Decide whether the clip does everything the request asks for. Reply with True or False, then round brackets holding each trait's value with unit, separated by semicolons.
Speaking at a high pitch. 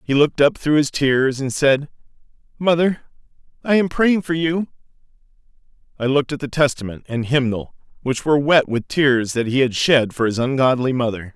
False (135 Hz)